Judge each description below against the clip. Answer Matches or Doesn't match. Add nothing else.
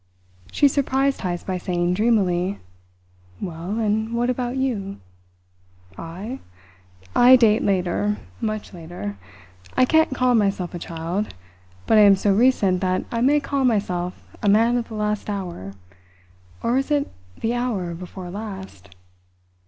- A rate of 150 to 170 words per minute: Doesn't match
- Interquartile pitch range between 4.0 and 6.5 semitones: Matches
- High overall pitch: Matches